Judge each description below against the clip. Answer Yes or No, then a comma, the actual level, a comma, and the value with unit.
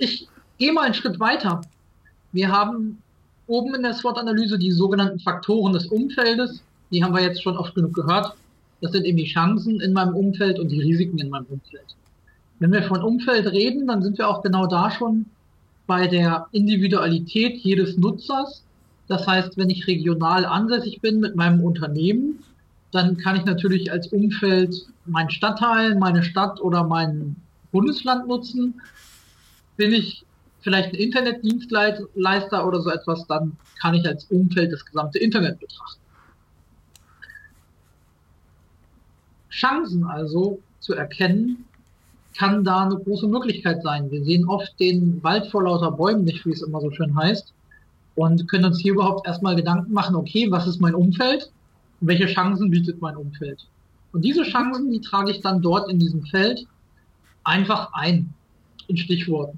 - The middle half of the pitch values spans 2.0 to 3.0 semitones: No, average, 4.0 semitones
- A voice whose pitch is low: No, medium, 185 Hz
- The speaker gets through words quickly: No, average, 155 wpm